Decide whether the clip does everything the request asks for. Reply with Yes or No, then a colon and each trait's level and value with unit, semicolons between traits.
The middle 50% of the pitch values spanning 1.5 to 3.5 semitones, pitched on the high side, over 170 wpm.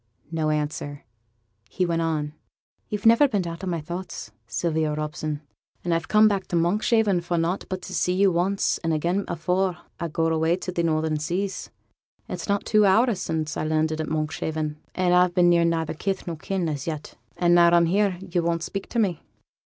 No: average, 3.0 semitones; medium, 170 Hz; average, 195 wpm